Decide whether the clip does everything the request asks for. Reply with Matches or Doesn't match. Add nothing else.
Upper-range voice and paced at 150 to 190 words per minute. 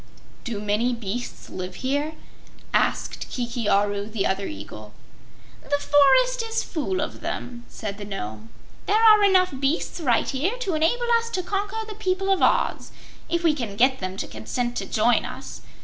Matches